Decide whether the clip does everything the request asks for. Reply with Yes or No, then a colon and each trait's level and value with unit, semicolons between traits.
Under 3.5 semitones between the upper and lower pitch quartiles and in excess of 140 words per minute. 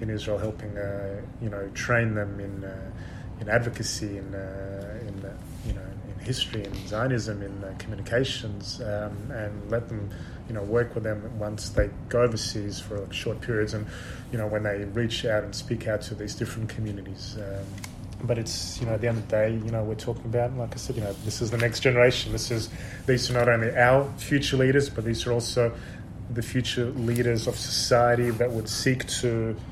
Yes: average, 2.8 semitones; fast, 205 wpm